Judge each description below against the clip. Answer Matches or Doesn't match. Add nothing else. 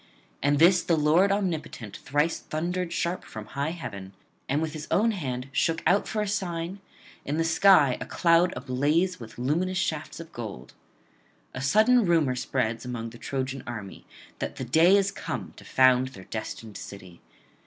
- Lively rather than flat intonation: Matches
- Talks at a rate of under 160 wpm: Doesn't match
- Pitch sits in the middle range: Matches